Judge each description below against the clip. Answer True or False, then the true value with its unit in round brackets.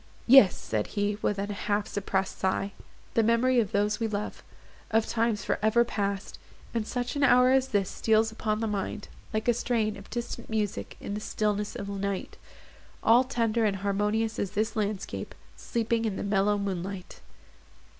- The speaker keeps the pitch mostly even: True (2.3 semitones)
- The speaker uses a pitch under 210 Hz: False (215 Hz)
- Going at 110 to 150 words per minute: False (165 wpm)